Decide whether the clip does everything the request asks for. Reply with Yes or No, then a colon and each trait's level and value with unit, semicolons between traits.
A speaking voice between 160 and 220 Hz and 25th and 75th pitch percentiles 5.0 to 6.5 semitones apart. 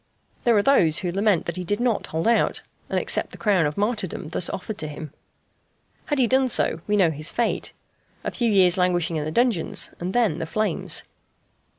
Yes: high, 190 Hz; wide, 5.4 semitones